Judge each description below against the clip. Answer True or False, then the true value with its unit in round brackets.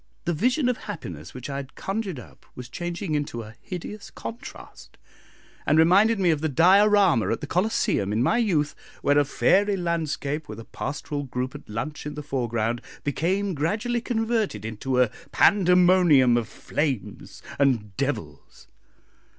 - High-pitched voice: False (155 Hz)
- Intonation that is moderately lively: False (7.5 semitones)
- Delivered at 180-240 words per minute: False (155 wpm)